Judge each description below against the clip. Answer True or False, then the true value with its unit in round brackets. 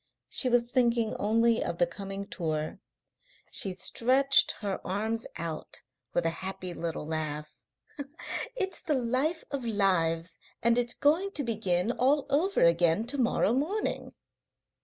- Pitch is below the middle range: False (225 Hz)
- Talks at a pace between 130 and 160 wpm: True (140 wpm)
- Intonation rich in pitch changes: True (6.8 semitones)